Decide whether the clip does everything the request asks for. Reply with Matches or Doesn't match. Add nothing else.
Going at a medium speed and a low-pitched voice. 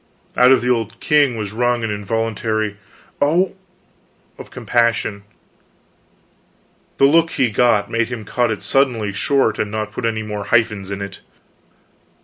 Matches